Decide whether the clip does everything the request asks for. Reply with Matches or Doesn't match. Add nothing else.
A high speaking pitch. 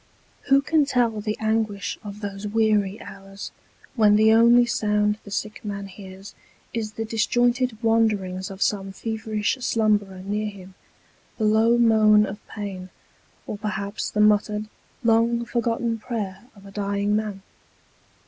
Matches